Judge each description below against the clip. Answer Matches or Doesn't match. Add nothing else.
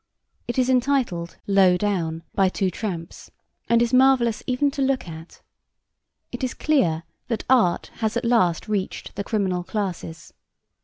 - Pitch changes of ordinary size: Doesn't match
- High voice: Matches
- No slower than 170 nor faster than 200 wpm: Doesn't match